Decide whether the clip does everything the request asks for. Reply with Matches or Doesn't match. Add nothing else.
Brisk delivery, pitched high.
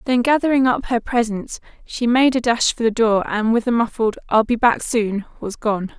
Matches